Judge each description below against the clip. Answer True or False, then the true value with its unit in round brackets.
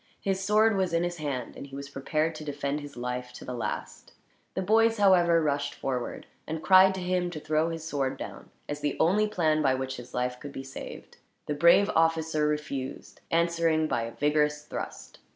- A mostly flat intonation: False (3.8 semitones)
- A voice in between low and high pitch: True (155 Hz)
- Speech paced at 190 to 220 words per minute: True (200 wpm)